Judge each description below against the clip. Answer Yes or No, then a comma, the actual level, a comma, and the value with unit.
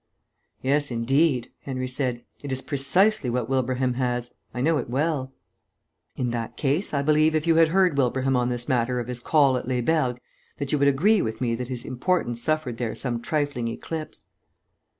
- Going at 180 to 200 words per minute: Yes, average, 190 wpm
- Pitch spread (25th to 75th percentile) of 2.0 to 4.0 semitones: Yes, average, 3.6 semitones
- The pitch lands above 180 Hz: No, low, 130 Hz